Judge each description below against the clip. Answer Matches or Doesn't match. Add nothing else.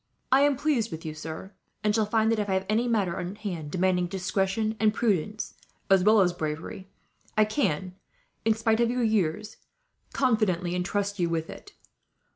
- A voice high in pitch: Matches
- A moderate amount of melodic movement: Matches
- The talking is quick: Doesn't match